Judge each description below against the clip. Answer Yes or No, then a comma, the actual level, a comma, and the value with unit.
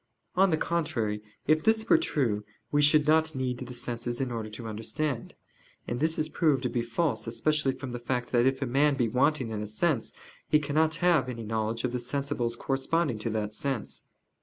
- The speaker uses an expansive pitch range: No, average, 4.6 semitones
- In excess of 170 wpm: Yes, fast, 205 wpm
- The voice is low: Yes, low, 130 Hz